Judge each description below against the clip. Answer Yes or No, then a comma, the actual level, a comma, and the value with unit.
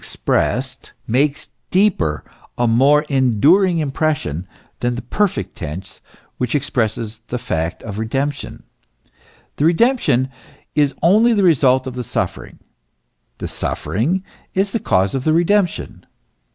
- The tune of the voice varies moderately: No, wide, 6.6 semitones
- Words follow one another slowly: Yes, slow, 125 wpm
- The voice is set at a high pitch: No, low, 135 Hz